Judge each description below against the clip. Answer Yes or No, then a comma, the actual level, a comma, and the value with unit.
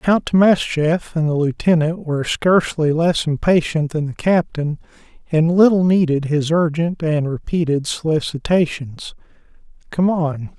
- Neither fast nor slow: No, slow, 125 wpm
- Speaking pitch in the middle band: Yes, medium, 160 Hz